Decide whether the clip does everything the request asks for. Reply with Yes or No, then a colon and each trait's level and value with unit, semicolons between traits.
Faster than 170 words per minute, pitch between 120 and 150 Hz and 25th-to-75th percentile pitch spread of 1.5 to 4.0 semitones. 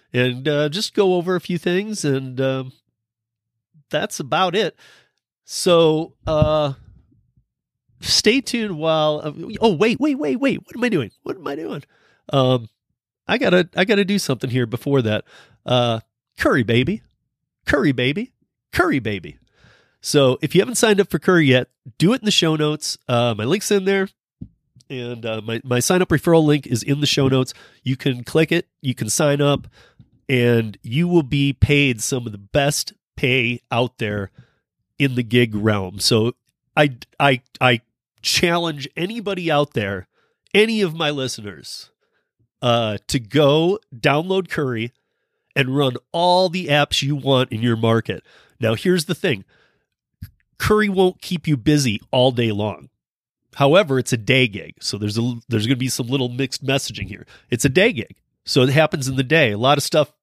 No: average, 180 wpm; medium, 140 Hz; wide, 5.5 semitones